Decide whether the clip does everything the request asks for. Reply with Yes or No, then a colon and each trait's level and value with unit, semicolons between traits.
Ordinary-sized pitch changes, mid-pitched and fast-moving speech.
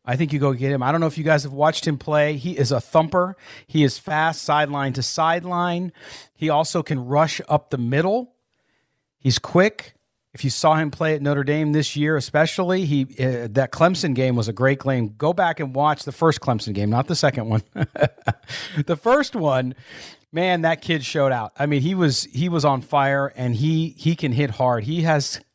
Yes: average, 3.3 semitones; medium, 150 Hz; fast, 215 wpm